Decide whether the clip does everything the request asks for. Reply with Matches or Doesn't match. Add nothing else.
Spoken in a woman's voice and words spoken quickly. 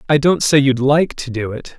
Doesn't match